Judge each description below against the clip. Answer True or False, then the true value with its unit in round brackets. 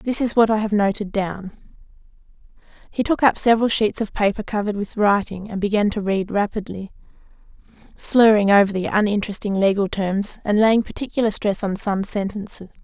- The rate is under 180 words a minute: True (165 wpm)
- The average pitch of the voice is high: True (205 Hz)